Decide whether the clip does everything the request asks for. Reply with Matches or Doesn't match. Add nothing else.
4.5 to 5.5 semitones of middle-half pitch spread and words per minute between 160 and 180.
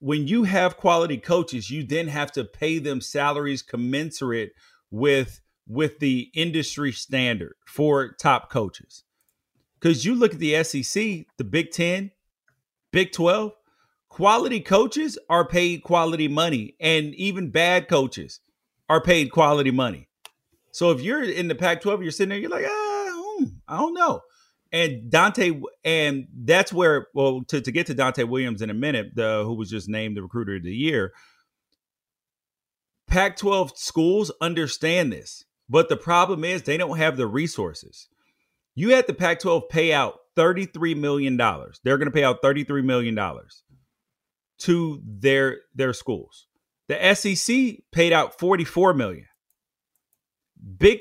Doesn't match